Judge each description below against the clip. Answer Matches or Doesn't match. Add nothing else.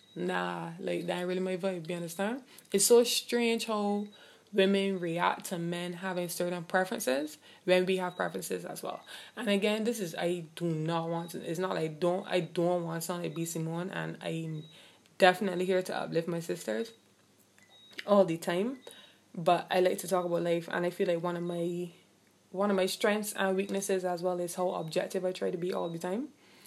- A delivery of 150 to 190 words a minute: Doesn't match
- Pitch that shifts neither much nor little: Doesn't match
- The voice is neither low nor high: Matches